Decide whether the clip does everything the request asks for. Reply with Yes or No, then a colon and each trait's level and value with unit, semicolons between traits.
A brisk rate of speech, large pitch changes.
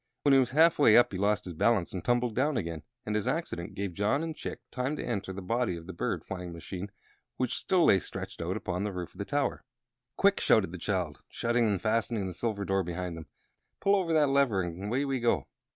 Yes: fast, 230 wpm; wide, 5.9 semitones